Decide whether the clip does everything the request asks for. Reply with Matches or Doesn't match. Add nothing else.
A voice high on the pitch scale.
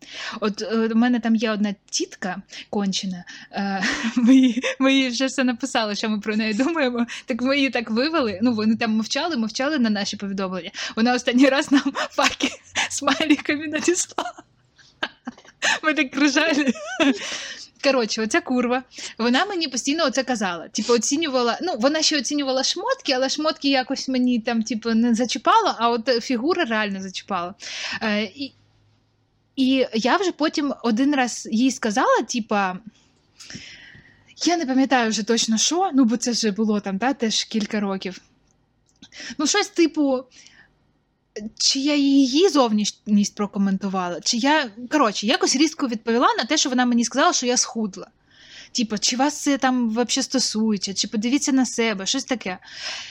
Matches